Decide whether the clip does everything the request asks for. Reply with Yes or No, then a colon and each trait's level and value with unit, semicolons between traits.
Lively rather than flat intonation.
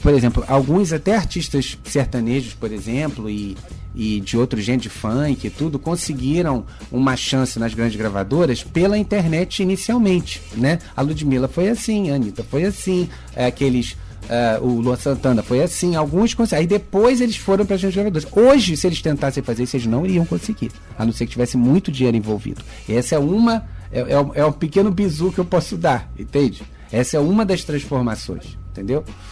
Yes: wide, 7.1 semitones